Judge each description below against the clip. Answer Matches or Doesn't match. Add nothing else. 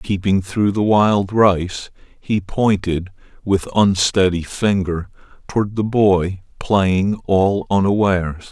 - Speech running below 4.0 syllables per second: Matches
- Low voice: Matches